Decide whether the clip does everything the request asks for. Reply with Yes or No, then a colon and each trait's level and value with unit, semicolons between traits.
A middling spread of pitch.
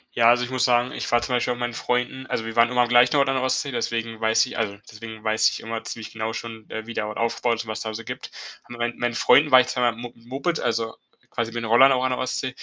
No: narrow, 1.8 semitones